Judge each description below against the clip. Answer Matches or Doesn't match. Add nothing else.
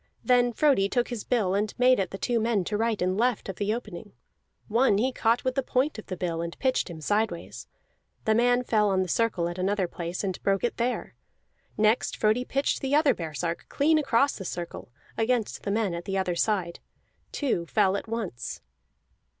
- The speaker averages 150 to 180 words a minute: Doesn't match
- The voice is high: Matches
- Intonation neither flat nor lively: Matches